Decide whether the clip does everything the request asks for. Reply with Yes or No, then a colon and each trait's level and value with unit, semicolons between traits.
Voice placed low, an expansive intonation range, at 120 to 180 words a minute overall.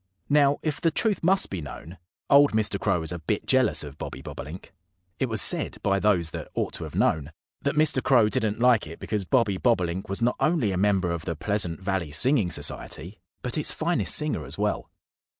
No: low, 105 Hz; wide, 7.2 semitones; fast, 205 wpm